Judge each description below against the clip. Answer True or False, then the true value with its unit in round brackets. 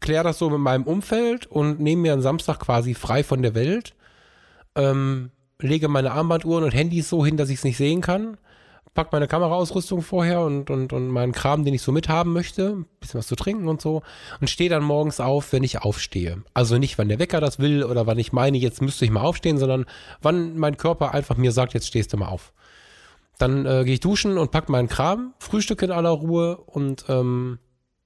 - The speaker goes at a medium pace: False (215 wpm)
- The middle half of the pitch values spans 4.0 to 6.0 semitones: True (4.6 semitones)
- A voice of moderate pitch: True (145 Hz)